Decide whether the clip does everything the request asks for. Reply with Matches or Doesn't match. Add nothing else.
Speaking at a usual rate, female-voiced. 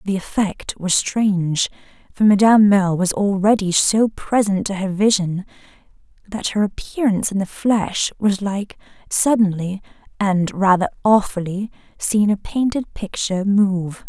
Doesn't match